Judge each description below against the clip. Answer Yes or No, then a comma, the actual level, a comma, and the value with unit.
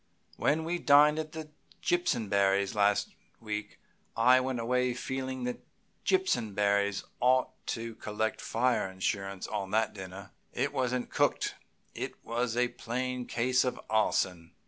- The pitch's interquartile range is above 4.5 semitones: No, average, 4.0 semitones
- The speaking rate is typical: No, slow, 125 wpm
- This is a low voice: Yes, low, 120 Hz